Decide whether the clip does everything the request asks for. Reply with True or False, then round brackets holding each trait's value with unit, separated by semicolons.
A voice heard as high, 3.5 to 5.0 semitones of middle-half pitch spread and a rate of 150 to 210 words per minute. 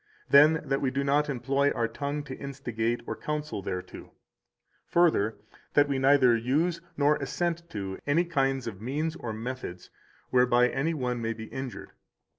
False (135 Hz; 3.8 semitones; 160 wpm)